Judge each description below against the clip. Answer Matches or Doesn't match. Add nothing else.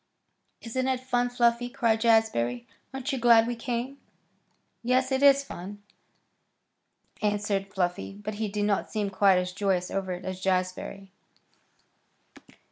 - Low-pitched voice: Doesn't match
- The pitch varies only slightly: Doesn't match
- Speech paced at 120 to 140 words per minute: Matches